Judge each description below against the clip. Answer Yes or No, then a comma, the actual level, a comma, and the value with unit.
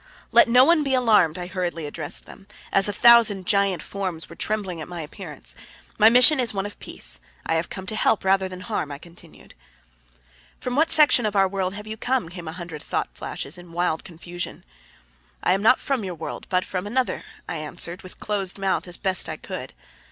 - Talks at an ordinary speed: No, fast, 210 wpm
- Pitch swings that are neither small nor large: Yes, average, 3.8 semitones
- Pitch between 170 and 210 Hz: Yes, high, 190 Hz